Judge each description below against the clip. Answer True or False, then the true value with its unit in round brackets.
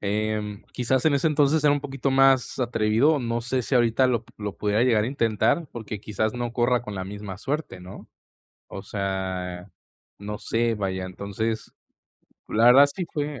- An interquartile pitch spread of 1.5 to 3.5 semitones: False (4.3 semitones)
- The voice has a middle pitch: False (115 Hz)